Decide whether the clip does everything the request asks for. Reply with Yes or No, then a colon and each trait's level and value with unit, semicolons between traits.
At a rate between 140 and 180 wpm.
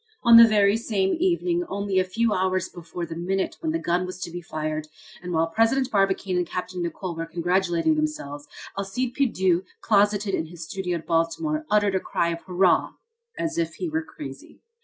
No: average, 190 wpm